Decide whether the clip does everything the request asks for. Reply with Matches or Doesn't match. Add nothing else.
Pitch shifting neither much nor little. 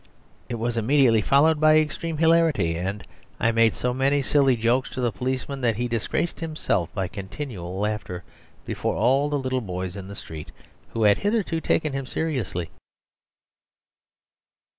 Doesn't match